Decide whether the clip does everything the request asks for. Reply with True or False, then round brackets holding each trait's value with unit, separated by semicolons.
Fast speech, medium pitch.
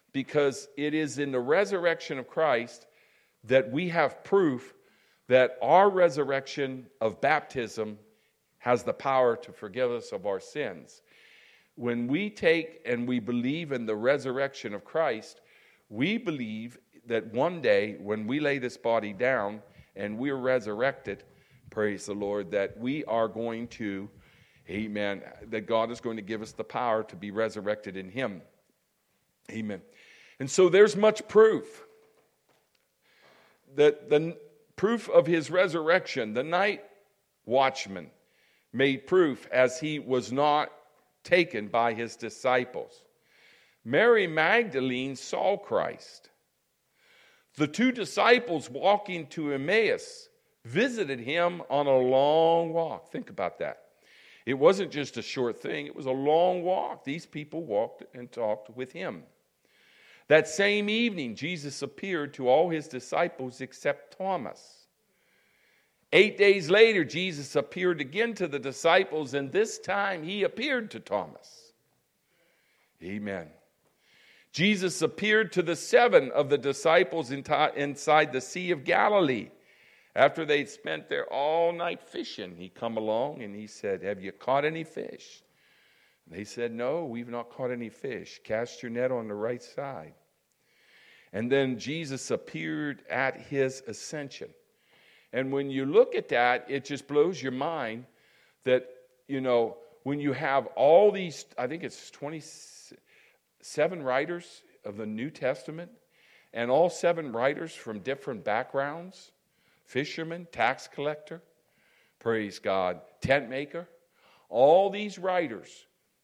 False (135 wpm; 145 Hz)